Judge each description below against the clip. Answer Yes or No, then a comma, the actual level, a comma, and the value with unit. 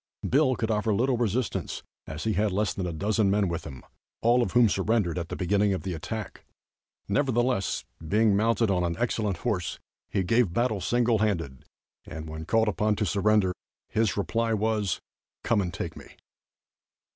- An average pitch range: Yes, average, 3.5 semitones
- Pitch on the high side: No, low, 105 Hz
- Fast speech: No, average, 175 wpm